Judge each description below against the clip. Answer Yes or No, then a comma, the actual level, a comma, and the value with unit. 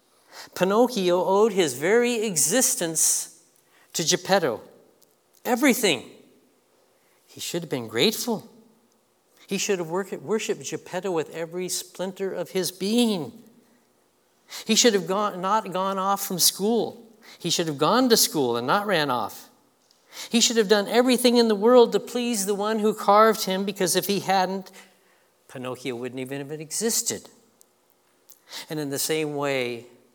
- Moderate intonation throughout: Yes, average, 4.4 semitones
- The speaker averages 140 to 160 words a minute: Yes, average, 145 wpm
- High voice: Yes, high, 200 Hz